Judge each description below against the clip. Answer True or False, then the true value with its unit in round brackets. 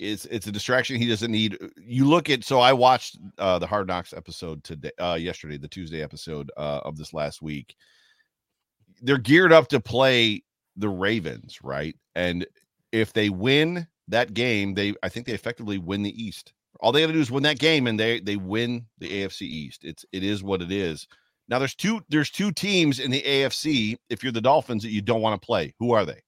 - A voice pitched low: True (110 Hz)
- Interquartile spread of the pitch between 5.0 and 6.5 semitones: True (5.5 semitones)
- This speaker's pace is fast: True (215 wpm)